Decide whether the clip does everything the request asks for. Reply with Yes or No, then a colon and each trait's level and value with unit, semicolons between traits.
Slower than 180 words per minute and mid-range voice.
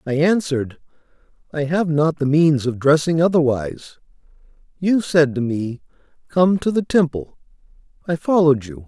Yes: average, 140 wpm; medium, 155 Hz